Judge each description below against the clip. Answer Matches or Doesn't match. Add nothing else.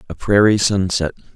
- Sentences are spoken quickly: Doesn't match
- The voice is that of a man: Matches